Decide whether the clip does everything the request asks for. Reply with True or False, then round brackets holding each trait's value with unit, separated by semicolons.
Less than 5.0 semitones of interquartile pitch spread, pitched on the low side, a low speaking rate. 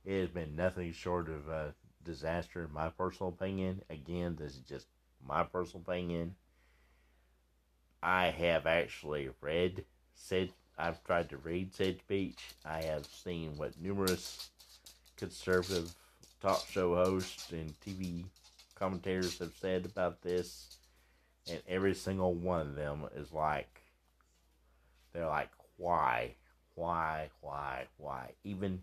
False (5.5 semitones; 85 Hz; 130 wpm)